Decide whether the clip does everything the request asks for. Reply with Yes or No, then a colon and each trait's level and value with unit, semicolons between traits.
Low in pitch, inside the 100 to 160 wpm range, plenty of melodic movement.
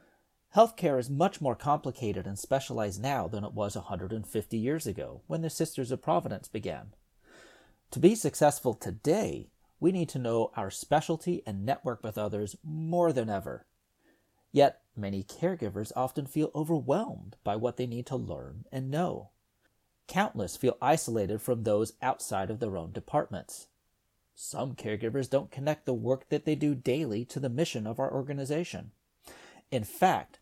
Yes: low, 130 Hz; average, 155 wpm; wide, 5.8 semitones